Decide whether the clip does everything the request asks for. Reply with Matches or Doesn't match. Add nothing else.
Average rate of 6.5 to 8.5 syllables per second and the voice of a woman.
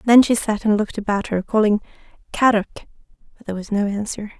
Matches